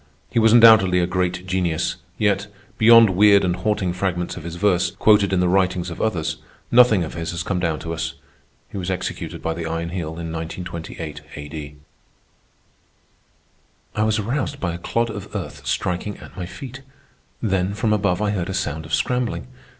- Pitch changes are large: No, average, 3.9 semitones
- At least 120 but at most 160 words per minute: No, average, 180 wpm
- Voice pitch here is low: Yes, very low, 90 Hz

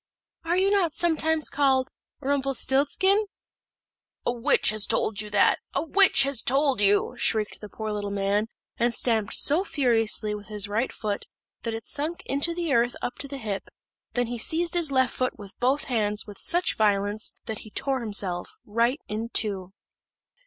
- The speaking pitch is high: Yes, high, 240 Hz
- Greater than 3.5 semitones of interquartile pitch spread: Yes, average, 5.3 semitones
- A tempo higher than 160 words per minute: Yes, average, 175 wpm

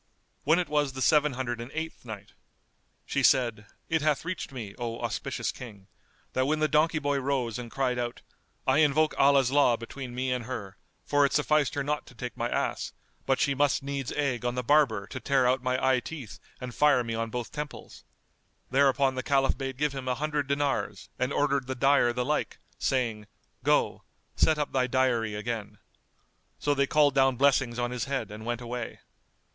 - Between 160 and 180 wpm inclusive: No, average, 195 wpm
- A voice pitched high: No, low, 130 Hz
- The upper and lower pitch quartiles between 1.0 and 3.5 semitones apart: Yes, average, 2.9 semitones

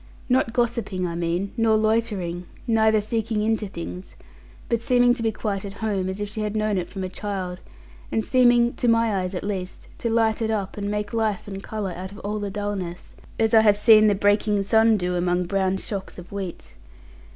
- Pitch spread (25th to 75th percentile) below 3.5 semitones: Yes, average, 2.8 semitones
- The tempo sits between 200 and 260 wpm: Yes, fast, 205 wpm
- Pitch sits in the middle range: No, high, 205 Hz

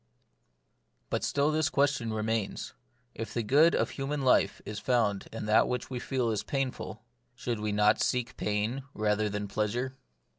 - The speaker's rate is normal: Yes, average, 160 wpm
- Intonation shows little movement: No, average, 3.9 semitones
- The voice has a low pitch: Yes, low, 115 Hz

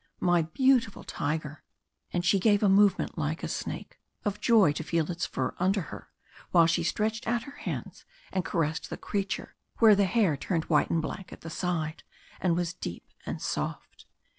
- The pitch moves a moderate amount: Yes, average, 4.0 semitones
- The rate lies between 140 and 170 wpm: No, average, 185 wpm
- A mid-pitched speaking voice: Yes, medium, 180 Hz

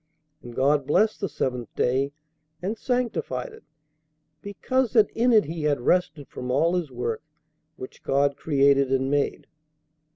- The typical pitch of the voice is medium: Yes, medium, 145 Hz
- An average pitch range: No, wide, 7.2 semitones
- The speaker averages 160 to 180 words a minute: No, average, 150 wpm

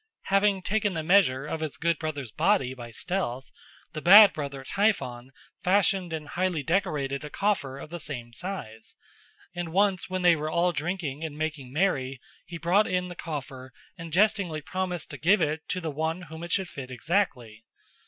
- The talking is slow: No, average, 180 wpm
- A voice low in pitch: No, medium, 165 Hz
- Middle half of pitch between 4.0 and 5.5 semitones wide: Yes, average, 5.0 semitones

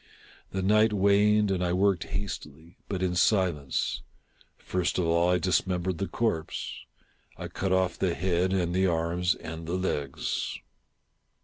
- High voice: No, very low, 90 Hz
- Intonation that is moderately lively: No, narrow, 2.0 semitones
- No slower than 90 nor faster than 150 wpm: Yes, average, 145 wpm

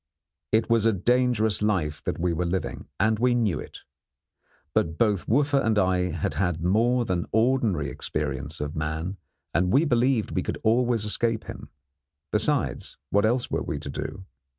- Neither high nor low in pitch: No, low, 105 Hz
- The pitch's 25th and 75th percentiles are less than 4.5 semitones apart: No, average, 5.2 semitones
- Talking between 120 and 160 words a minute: No, average, 170 wpm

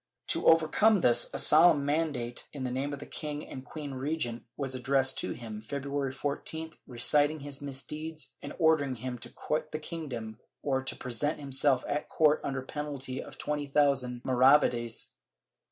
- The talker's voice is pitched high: No, medium, 140 Hz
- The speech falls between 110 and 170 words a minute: Yes, average, 165 wpm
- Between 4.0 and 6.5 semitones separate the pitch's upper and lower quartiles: No, average, 2.7 semitones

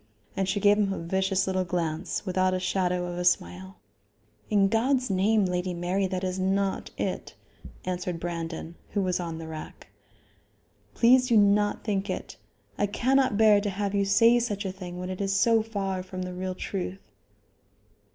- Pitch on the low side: No, high, 190 Hz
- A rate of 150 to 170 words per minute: No, average, 180 wpm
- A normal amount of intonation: No, narrow, 2.2 semitones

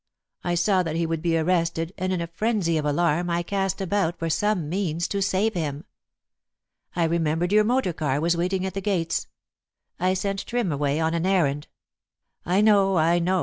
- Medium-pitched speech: Yes, medium, 175 Hz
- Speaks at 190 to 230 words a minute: Yes, average, 195 wpm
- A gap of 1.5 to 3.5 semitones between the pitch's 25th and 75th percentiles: Yes, average, 2.8 semitones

